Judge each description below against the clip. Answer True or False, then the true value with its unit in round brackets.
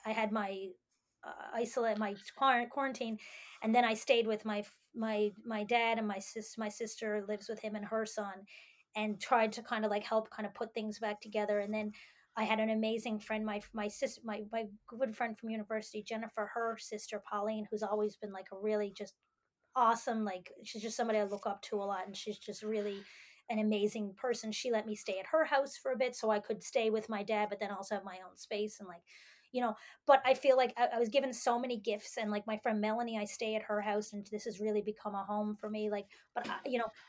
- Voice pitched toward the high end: True (215 Hz)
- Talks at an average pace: False (240 wpm)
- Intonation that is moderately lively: False (1.6 semitones)